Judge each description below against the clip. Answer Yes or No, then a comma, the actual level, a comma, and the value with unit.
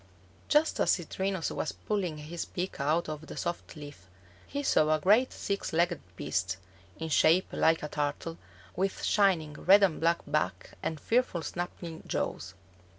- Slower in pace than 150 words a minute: No, average, 155 wpm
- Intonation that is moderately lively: Yes, average, 3.8 semitones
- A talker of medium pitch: Yes, medium, 165 Hz